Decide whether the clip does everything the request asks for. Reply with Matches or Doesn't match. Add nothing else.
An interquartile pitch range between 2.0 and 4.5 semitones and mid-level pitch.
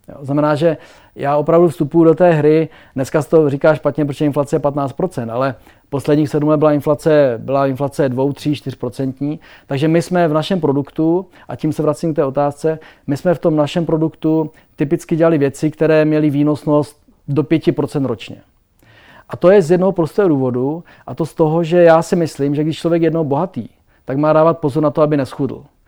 Matches